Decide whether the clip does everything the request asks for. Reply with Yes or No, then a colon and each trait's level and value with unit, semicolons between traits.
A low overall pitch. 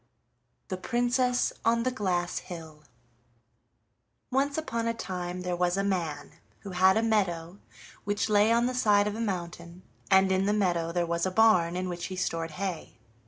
No: high, 190 Hz